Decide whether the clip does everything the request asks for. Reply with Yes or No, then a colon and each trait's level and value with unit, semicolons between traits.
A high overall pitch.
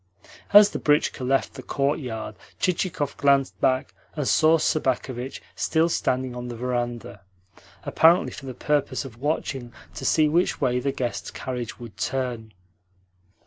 No: low, 130 Hz